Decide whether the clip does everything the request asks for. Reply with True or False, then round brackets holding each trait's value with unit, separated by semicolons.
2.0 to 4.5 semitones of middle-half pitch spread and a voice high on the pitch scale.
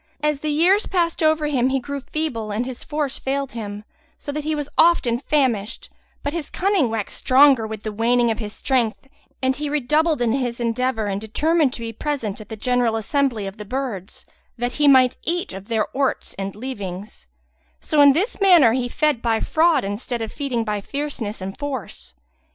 False (4.9 semitones; 255 Hz)